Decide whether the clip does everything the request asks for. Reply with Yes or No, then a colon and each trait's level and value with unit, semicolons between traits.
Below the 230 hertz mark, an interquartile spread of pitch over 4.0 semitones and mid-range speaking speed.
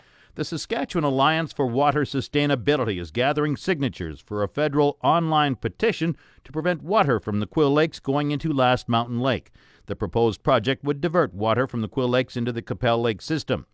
Yes: low, 135 Hz; average, 4.4 semitones; average, 180 wpm